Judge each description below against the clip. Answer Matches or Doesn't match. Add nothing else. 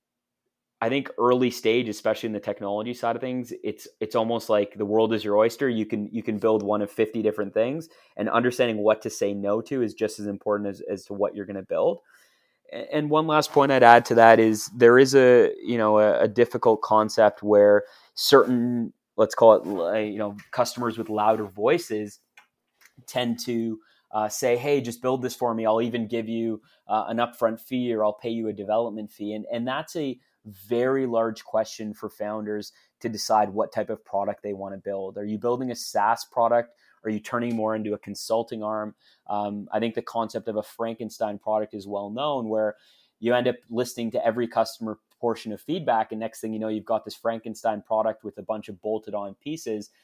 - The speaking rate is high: Matches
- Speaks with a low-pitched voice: Matches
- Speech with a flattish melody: Matches